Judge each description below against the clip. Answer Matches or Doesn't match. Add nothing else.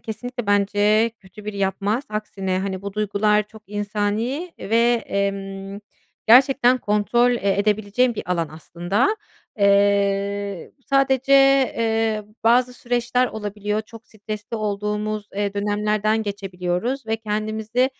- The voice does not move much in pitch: Matches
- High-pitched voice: Matches